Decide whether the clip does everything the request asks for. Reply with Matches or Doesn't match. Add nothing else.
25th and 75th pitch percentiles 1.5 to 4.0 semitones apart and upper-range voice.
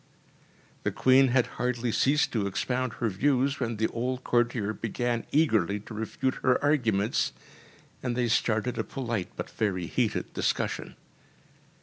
Doesn't match